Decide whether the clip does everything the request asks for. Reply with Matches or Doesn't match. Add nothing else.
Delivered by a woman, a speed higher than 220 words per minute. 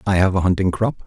Doesn't match